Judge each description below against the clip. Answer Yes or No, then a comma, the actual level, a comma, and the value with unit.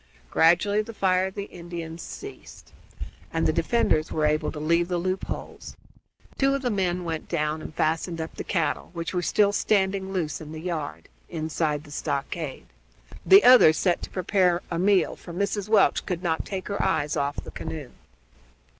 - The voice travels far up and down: No, average, 3.5 semitones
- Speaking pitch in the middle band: Yes, medium, 175 Hz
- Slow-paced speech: No, average, 185 wpm